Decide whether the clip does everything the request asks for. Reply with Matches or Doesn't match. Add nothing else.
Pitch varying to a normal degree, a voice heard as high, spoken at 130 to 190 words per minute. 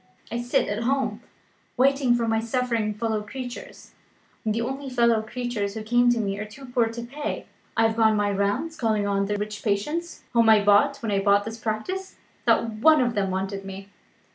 Doesn't match